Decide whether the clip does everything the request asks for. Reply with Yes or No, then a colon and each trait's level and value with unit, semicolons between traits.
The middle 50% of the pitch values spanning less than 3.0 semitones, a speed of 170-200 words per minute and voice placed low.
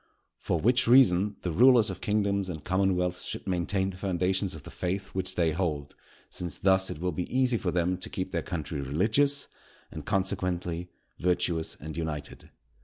Yes: narrow, 2.5 semitones; average, 175 wpm; very low, 90 Hz